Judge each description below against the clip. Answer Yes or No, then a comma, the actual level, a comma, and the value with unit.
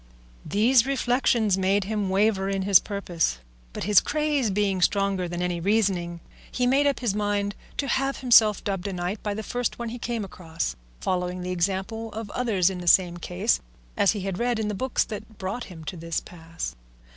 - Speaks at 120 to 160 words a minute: No, average, 195 wpm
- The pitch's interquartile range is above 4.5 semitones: No, average, 3.7 semitones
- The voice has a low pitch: No, high, 200 Hz